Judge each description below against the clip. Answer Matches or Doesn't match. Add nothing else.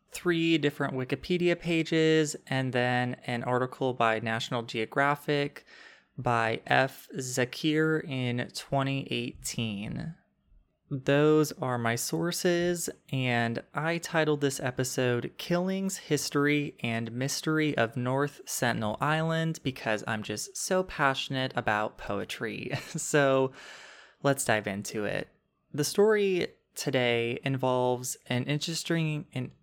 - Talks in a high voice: Doesn't match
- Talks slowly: Matches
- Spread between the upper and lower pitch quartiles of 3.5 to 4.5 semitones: Matches